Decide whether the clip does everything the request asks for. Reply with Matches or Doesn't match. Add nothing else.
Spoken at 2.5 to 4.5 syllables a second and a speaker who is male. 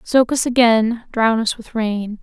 Doesn't match